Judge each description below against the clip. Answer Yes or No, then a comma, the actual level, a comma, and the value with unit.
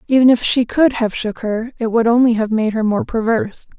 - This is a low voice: No, high, 230 Hz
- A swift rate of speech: Yes, fast, 240 wpm